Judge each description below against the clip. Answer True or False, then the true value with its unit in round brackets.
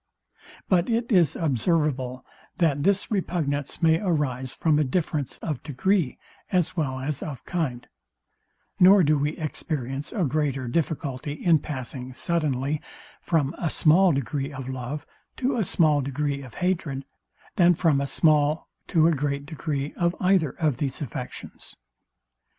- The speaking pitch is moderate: True (150 Hz)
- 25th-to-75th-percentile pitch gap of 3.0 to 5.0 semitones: True (3.8 semitones)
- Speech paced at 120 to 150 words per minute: True (145 wpm)